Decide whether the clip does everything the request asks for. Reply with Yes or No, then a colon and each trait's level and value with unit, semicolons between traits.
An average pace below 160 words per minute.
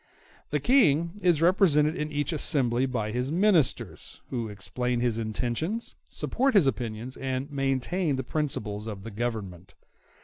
Yes: average, 140 wpm